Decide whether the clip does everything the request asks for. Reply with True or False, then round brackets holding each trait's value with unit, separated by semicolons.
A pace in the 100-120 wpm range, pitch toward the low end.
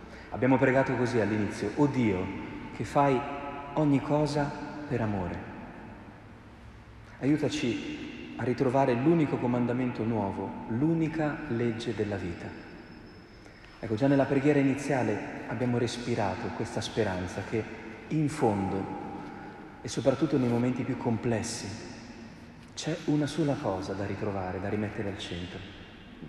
True (115 wpm; 120 Hz)